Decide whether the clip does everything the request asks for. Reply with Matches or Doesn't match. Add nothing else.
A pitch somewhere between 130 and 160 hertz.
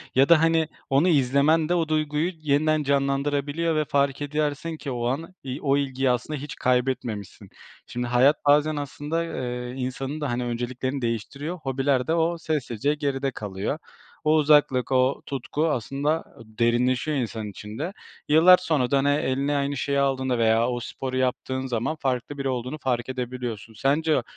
Matches